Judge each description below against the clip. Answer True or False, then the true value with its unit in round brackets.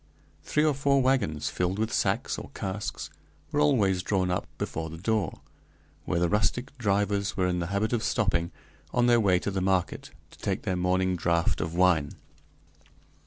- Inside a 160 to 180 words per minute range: True (175 wpm)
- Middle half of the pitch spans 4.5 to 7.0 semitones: False (3.8 semitones)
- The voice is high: False (95 Hz)